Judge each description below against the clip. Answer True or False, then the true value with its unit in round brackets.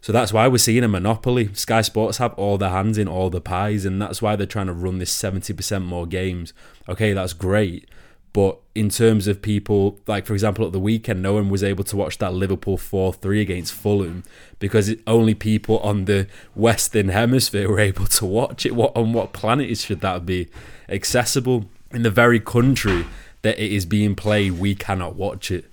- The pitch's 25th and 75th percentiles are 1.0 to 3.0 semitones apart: True (2.4 semitones)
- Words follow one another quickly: True (210 wpm)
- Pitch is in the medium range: False (105 Hz)